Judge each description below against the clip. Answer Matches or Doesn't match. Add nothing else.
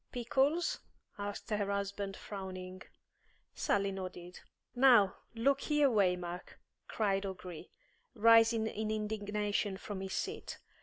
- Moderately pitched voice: Doesn't match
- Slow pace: Matches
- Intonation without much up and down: Doesn't match